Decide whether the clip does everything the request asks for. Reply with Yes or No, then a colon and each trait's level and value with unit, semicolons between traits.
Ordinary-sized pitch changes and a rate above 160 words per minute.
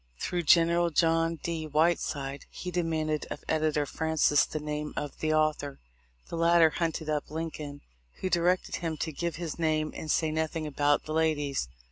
No: narrow, 1.7 semitones; average, 170 wpm